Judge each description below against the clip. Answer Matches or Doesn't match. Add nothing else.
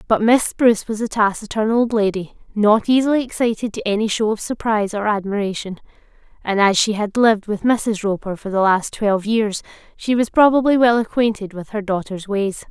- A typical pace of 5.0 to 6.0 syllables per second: Matches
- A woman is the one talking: Matches